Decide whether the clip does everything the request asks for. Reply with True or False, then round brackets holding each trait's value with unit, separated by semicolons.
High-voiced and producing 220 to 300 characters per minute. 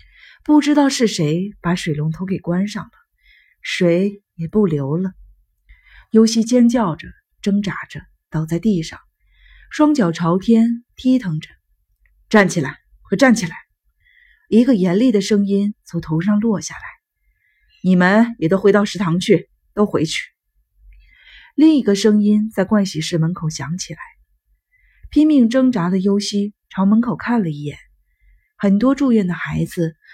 False (200 Hz; 205 characters per minute)